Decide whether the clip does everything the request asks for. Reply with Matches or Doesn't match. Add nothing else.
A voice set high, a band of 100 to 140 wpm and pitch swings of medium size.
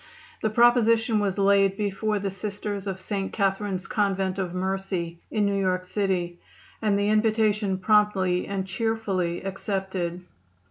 Doesn't match